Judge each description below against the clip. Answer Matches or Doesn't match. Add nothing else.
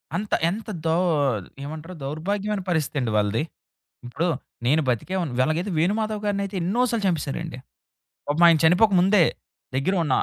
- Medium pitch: Matches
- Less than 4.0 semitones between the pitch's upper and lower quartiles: Doesn't match